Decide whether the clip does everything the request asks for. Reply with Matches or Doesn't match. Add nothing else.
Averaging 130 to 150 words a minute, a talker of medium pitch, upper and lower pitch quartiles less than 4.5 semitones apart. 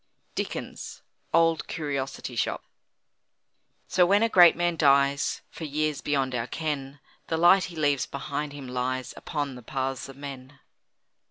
Matches